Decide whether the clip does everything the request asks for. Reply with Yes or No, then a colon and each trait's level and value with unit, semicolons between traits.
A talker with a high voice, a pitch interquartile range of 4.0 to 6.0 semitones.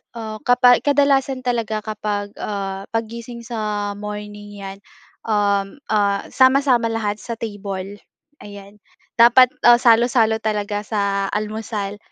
No: high, 215 Hz; narrow, 2.5 semitones